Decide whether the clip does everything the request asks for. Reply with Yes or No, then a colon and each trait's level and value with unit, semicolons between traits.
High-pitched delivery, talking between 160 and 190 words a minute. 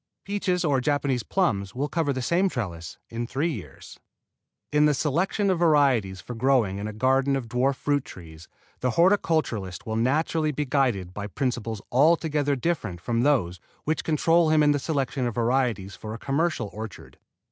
No: low, 135 Hz; average, 170 wpm